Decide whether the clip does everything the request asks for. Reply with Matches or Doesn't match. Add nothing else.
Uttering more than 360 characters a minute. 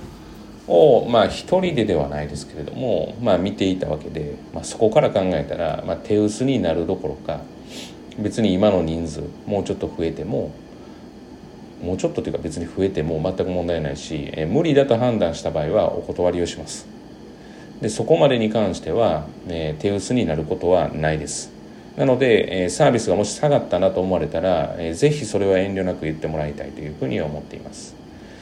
Matches